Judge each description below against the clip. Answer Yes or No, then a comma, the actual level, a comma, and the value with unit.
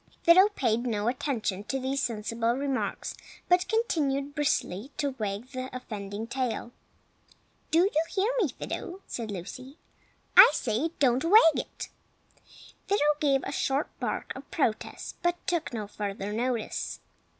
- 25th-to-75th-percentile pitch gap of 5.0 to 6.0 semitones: Yes, wide, 5.4 semitones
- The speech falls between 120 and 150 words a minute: Yes, average, 140 wpm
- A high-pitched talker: Yes, very high, 260 Hz